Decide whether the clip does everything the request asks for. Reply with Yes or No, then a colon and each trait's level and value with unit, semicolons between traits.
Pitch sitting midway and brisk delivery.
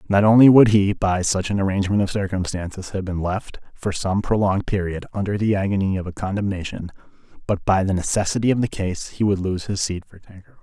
No: low, 100 Hz; fast, 210 wpm